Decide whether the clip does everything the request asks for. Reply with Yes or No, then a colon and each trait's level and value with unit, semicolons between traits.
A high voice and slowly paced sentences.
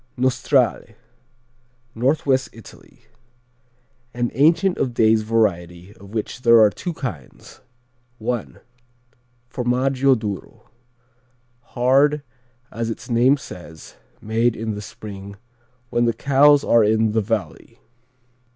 No: low, 115 Hz; slow, 105 wpm